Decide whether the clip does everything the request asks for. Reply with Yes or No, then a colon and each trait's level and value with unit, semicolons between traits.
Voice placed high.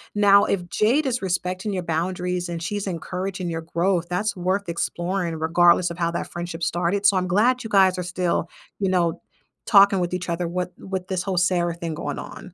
No: medium, 180 Hz